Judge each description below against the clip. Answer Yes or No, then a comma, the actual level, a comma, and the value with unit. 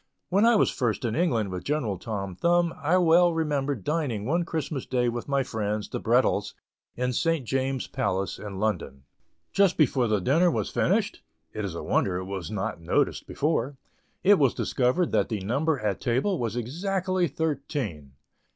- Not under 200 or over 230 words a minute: No, average, 175 wpm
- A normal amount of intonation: No, wide, 7.4 semitones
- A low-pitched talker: Yes, low, 130 Hz